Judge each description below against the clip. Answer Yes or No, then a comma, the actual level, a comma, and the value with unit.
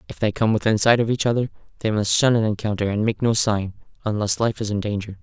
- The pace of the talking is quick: Yes, fast, 240 wpm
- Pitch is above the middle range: No, low, 110 Hz